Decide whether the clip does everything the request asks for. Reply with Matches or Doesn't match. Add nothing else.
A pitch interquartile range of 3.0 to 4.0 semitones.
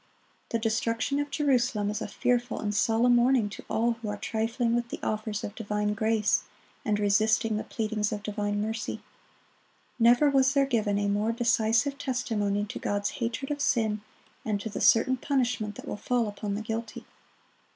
Doesn't match